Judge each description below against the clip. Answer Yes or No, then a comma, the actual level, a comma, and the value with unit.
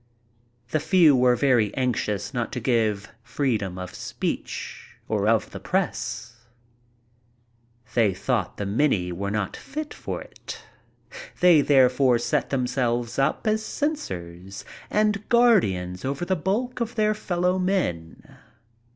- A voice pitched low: Yes, low, 125 Hz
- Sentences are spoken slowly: Yes, slow, 125 wpm